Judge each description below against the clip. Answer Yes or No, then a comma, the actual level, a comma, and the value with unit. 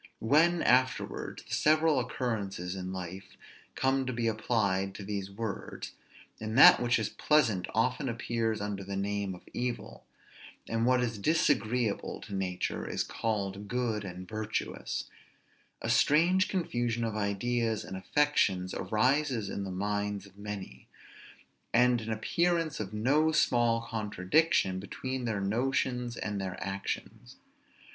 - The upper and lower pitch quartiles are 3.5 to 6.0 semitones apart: Yes, average, 4.1 semitones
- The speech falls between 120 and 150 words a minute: Yes, slow, 135 wpm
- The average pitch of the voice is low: Yes, low, 110 Hz